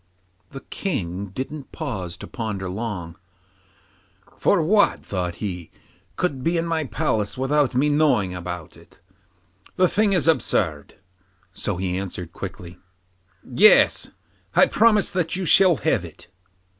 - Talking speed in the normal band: No, slow, 130 wpm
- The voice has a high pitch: No, low, 120 Hz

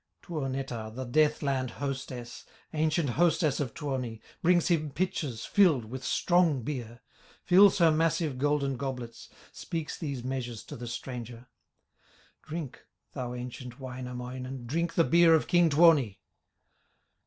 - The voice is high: No, low, 135 Hz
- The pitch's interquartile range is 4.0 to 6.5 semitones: Yes, average, 4.4 semitones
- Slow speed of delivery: Yes, slow, 130 wpm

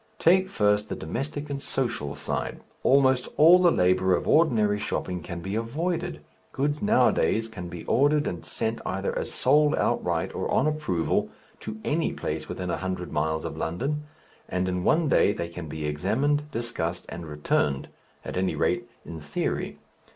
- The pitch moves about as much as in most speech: No, wide, 8.8 semitones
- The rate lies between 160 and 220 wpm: Yes, average, 165 wpm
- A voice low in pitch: Yes, low, 110 Hz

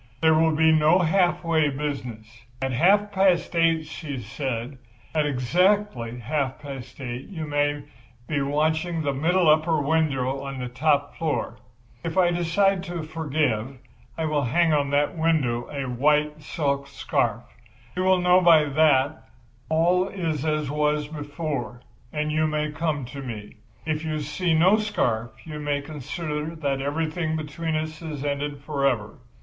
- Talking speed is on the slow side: No, average, 160 wpm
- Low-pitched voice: No, medium, 150 Hz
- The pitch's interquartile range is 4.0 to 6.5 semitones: No, average, 2.7 semitones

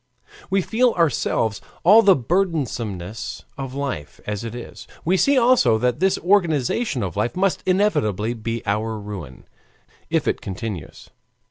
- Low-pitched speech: Yes, low, 125 Hz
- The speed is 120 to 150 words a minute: Yes, average, 140 wpm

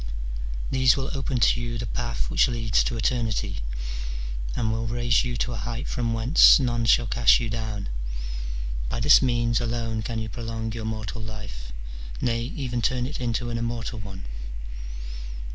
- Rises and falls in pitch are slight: Yes, narrow, 1.4 semitones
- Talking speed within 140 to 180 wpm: Yes, average, 165 wpm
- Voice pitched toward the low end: Yes, low, 115 Hz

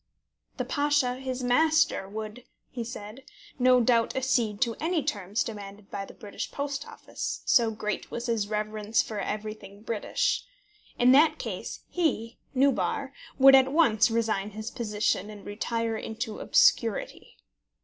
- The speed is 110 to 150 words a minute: Yes, average, 140 wpm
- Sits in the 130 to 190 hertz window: No, high, 230 Hz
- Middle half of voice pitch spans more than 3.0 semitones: Yes, average, 3.8 semitones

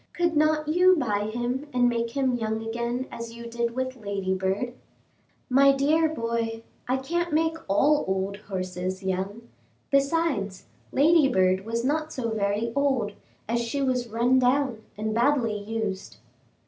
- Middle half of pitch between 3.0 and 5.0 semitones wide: Yes, average, 4.7 semitones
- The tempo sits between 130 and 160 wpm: Yes, average, 145 wpm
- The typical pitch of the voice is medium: No, high, 235 Hz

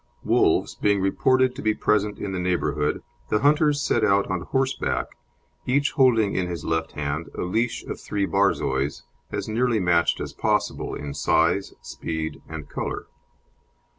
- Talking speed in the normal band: Yes, average, 155 wpm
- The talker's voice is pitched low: Yes, low, 100 Hz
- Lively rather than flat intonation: Yes, wide, 6.2 semitones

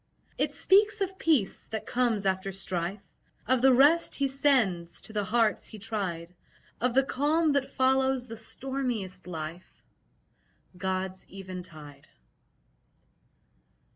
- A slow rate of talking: Yes, slow, 120 wpm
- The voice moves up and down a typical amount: No, wide, 6.2 semitones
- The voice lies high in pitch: Yes, high, 220 Hz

